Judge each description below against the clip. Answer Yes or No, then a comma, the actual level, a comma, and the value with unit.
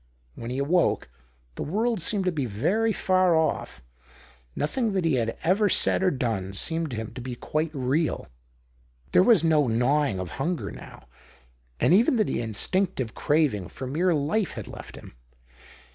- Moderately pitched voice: Yes, medium, 155 Hz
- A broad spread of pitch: Yes, wide, 6.8 semitones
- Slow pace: No, average, 165 wpm